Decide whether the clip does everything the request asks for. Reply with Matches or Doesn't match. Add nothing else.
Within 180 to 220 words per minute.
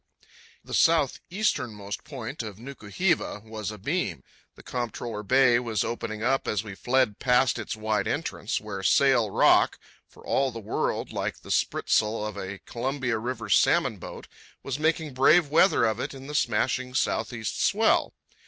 Doesn't match